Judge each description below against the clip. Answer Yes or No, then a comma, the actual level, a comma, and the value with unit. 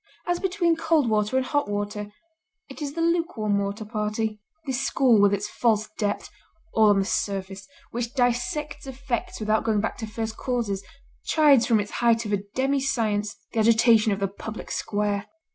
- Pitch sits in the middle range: No, high, 220 Hz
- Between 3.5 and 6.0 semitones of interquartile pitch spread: Yes, average, 4.2 semitones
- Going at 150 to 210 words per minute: Yes, average, 180 wpm